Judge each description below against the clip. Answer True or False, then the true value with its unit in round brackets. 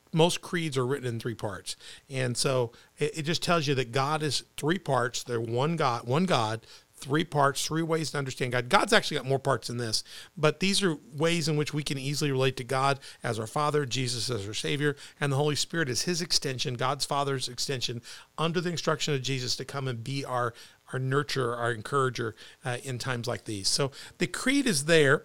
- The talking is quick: True (215 wpm)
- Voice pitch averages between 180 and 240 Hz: False (140 Hz)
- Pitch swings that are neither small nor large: True (3.9 semitones)